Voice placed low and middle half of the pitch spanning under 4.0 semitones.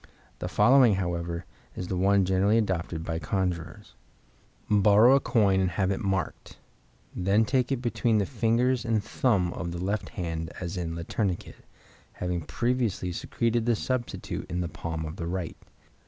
No: very low, 95 Hz; average, 4.6 semitones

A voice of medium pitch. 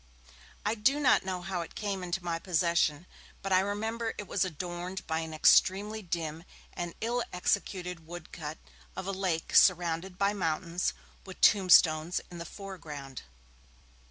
Yes: medium, 180 Hz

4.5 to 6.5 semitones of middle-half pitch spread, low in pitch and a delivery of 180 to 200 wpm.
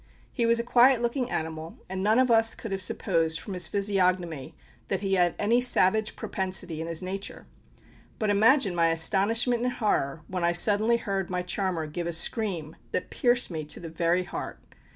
No: average, 4.8 semitones; high, 190 Hz; average, 190 wpm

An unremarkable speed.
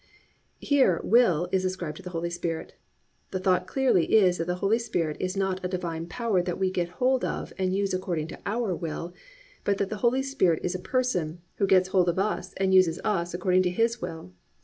No: fast, 215 wpm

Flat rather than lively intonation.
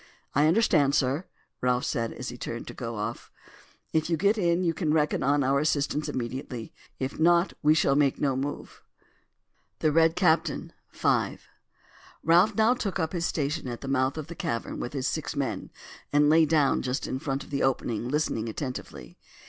No: average, 3.8 semitones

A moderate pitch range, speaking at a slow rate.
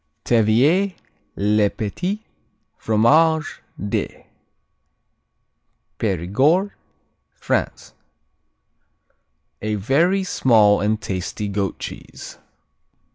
No: wide, 7.6 semitones; slow, 60 wpm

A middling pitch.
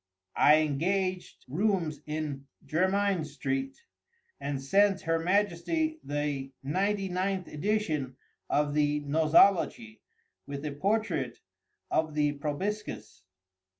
Yes: medium, 160 Hz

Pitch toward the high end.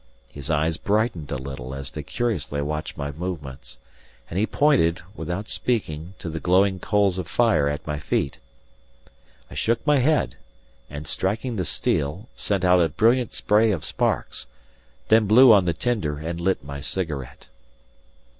No: very low, 90 Hz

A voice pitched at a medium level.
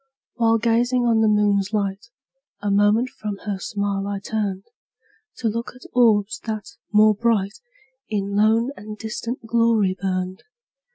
No: high, 215 Hz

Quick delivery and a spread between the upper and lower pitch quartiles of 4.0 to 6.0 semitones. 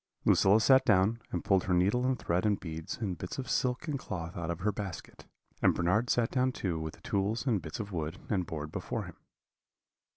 Yes: fast, 220 wpm; average, 5.1 semitones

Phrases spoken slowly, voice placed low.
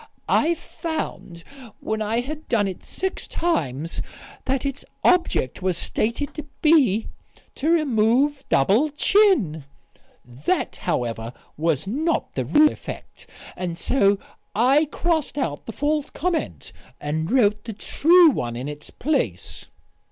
No: slow, 130 wpm; high, 240 Hz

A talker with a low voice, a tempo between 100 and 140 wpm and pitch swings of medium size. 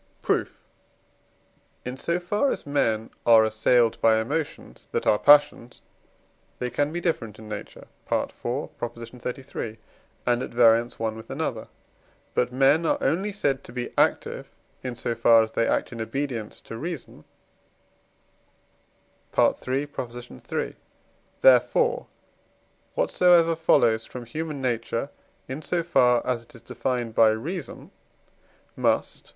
Yes: low, 125 Hz; slow, 135 wpm; average, 4.2 semitones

